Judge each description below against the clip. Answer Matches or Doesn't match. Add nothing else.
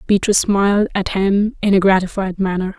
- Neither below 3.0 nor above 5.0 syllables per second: Doesn't match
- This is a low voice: Doesn't match